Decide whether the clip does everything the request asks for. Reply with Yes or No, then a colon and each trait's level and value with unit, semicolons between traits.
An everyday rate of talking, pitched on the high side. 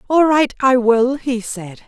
Yes: average, 190 wpm; very high, 250 Hz